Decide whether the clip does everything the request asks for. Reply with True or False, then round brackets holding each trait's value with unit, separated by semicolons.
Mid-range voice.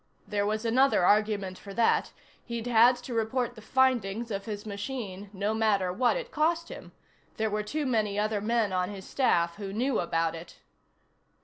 False (215 Hz)